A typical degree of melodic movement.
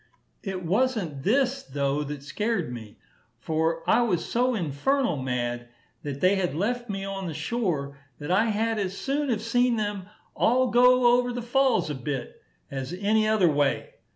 No: wide, 8.5 semitones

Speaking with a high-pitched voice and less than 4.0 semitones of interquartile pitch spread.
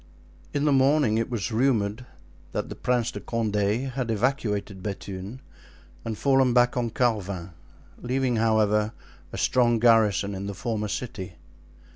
No: low, 115 Hz; average, 3.4 semitones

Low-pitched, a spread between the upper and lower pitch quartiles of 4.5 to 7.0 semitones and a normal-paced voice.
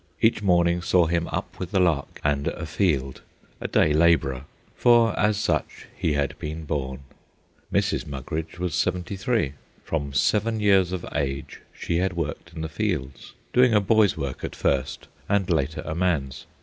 Yes: very low, 85 Hz; average, 5.1 semitones; average, 165 wpm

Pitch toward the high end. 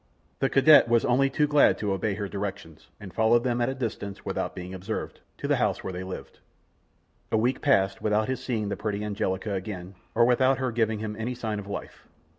No: low, 110 Hz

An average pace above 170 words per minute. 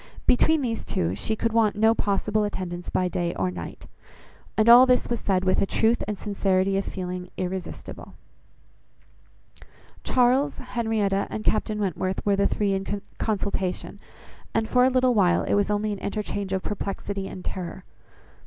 No: average, 160 wpm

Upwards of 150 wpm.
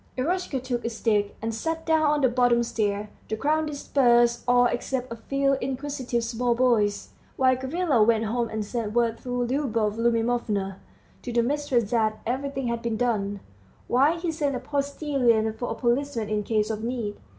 Yes: average, 175 wpm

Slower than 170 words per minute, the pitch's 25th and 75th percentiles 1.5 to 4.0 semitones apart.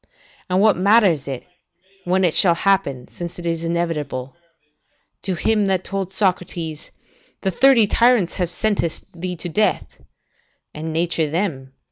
Yes: average, 150 wpm; average, 3.3 semitones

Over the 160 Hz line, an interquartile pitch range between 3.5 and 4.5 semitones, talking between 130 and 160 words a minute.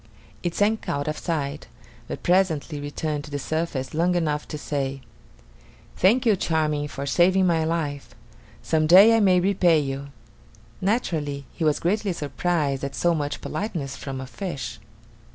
No: medium, 155 Hz; average, 3.9 semitones; average, 155 wpm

